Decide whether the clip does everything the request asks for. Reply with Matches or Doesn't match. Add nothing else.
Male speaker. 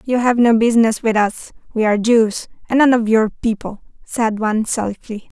Doesn't match